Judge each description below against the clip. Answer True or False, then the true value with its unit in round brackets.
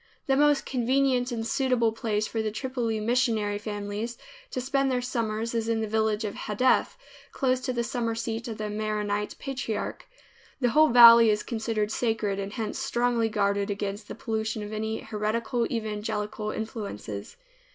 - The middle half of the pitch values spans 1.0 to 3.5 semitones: True (2.4 semitones)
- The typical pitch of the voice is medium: False (225 Hz)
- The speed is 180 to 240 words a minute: False (160 wpm)